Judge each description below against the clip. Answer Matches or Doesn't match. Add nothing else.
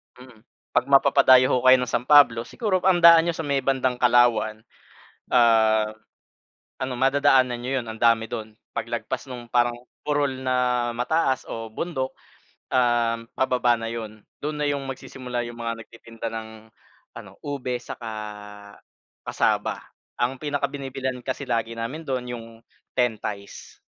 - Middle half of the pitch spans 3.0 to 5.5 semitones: Doesn't match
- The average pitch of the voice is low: Matches